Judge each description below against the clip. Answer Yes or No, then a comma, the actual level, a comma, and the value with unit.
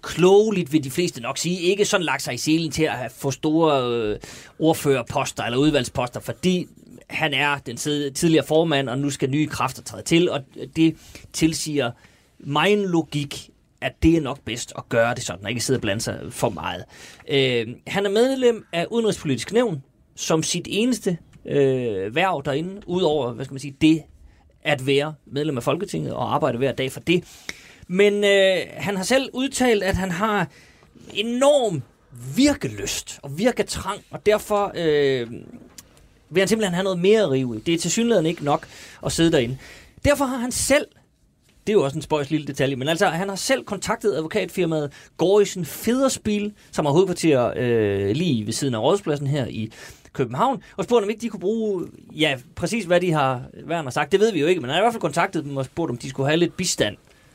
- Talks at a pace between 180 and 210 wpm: Yes, average, 190 wpm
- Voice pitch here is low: No, medium, 155 Hz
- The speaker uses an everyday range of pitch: No, wide, 6.0 semitones